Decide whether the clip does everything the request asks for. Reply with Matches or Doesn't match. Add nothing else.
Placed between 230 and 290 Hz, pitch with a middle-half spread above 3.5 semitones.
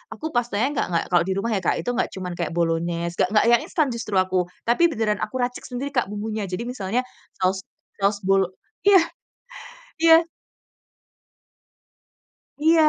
Doesn't match